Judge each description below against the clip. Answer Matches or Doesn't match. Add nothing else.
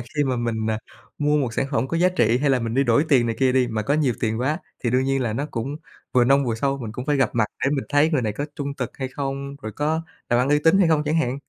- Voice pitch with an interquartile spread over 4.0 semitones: Doesn't match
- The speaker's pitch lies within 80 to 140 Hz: Matches